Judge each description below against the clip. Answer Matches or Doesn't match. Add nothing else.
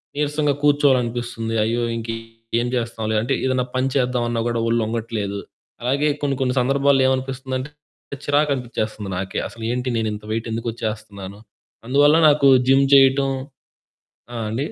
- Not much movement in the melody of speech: Doesn't match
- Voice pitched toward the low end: Matches